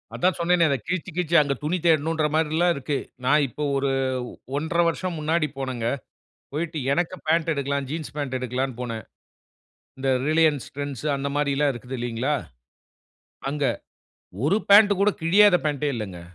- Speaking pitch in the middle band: Yes, medium, 150 Hz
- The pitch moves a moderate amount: Yes, average, 3.5 semitones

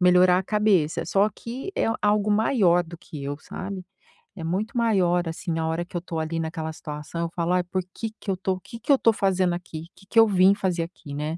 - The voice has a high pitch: No, medium, 180 Hz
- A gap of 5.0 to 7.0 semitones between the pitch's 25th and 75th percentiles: No, average, 3.5 semitones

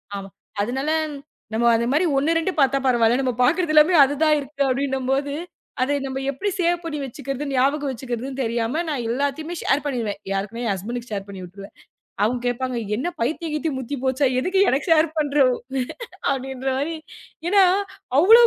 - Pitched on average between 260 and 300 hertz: Yes, very high, 270 Hz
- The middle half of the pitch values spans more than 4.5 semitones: No, average, 3.9 semitones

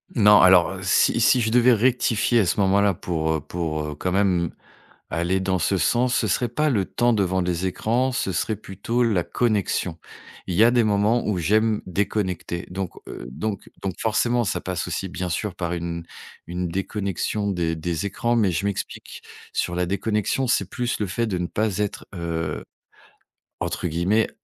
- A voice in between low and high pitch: No, very low, 95 Hz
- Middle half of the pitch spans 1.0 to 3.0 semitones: No, average, 3.8 semitones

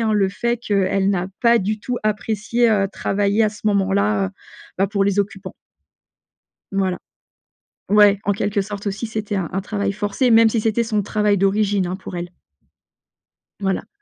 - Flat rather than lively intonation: Yes, narrow, 1.8 semitones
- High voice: Yes, high, 205 Hz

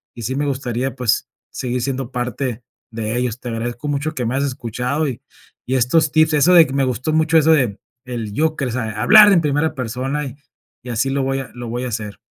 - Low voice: Yes, low, 130 Hz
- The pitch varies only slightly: No, average, 3.3 semitones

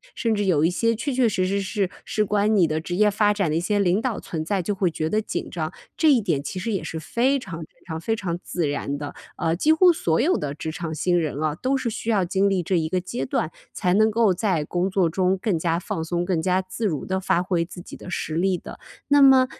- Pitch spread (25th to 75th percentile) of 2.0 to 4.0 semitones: No, average, 4.4 semitones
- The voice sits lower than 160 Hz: No, medium, 185 Hz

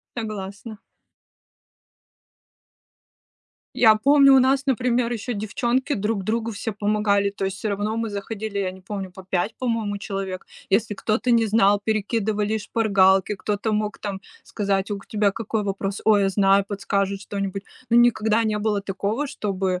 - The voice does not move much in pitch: Yes, narrow, 2.2 semitones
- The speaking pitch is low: No, high, 210 Hz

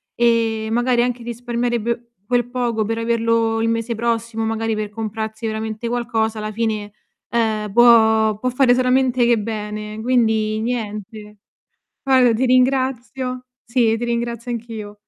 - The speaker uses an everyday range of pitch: No, narrow, 1.7 semitones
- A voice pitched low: No, high, 230 Hz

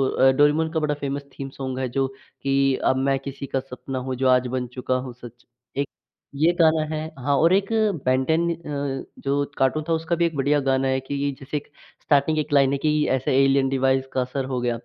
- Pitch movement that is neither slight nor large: No, narrow, 2.0 semitones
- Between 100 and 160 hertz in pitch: Yes, low, 135 Hz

